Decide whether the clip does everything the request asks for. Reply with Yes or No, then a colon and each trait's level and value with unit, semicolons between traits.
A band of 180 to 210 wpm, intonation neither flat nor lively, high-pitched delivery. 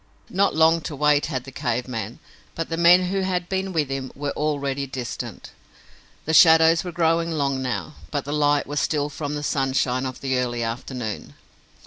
No: average, 185 wpm; average, 3.8 semitones; medium, 145 Hz